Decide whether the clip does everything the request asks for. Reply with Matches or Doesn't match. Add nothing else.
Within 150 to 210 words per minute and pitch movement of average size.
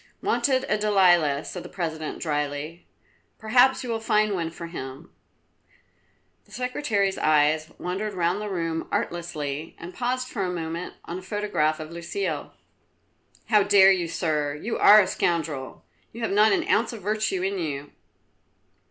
Matches